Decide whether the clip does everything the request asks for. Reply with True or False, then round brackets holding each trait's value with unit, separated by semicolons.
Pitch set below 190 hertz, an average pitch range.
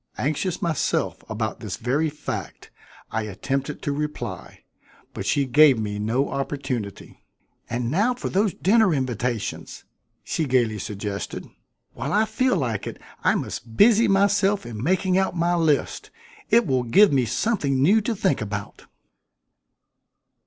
False (140 Hz; 8.3 semitones)